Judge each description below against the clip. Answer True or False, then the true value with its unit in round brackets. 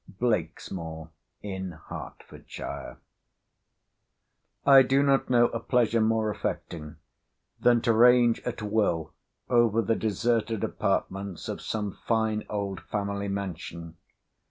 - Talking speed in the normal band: False (110 wpm)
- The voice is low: True (110 Hz)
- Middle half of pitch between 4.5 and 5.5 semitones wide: False (3.7 semitones)